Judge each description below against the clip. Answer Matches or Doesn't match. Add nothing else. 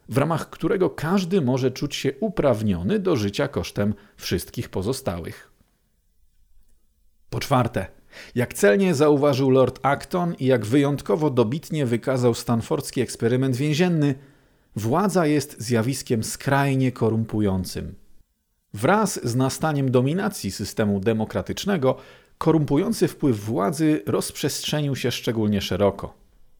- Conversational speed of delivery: Doesn't match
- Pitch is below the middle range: Matches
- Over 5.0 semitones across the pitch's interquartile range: Matches